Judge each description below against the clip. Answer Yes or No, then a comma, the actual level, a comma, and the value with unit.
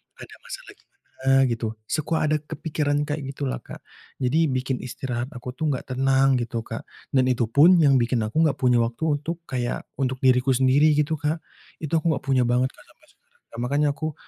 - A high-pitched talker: No, low, 135 Hz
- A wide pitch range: No, average, 3.4 semitones